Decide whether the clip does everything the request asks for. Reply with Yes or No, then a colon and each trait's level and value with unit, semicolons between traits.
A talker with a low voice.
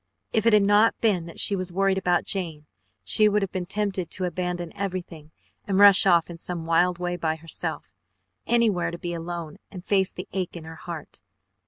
No: medium, 180 Hz